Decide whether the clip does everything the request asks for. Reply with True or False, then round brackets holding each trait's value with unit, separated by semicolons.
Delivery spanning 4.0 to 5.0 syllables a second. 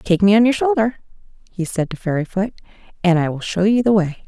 False (5.9 syllables/s)